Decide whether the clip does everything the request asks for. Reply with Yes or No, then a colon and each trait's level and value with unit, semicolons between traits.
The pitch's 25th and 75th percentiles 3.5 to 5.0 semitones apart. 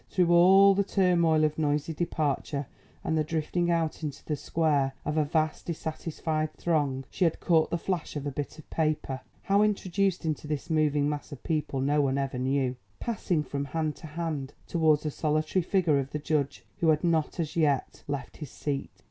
No: narrow, 2.6 semitones